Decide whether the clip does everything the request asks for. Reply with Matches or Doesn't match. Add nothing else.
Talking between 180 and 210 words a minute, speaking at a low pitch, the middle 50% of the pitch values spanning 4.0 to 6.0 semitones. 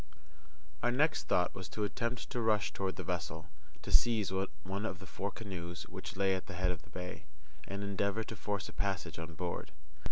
Doesn't match